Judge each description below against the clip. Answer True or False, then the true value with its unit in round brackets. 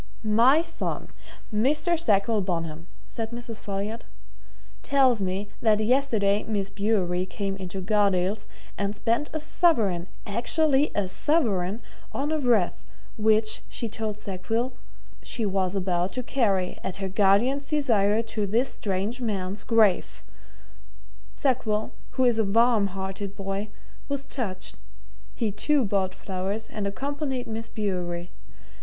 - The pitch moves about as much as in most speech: True (3.8 semitones)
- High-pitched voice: True (210 Hz)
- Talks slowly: True (130 wpm)